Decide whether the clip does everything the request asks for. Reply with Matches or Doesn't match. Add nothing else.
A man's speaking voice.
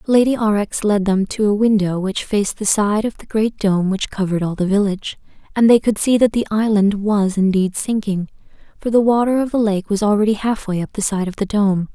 Doesn't match